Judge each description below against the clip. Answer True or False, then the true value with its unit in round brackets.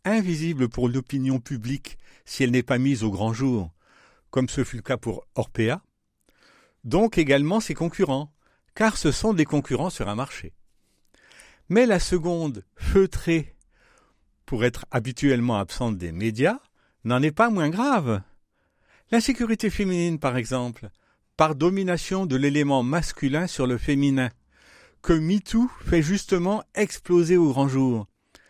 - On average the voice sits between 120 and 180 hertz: True (140 Hz)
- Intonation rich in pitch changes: True (6.1 semitones)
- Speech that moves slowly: True (140 wpm)